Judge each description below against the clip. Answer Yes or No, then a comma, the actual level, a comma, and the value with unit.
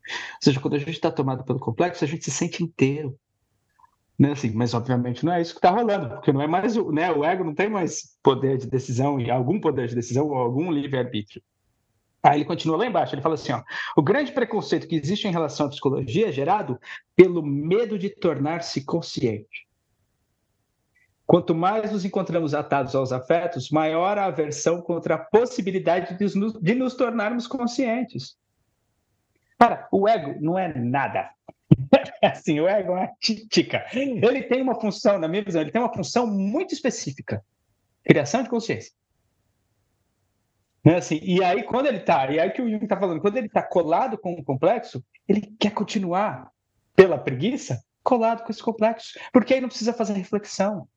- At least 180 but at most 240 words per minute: Yes, fast, 185 wpm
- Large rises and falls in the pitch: Yes, wide, 7.7 semitones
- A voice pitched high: No, medium, 170 Hz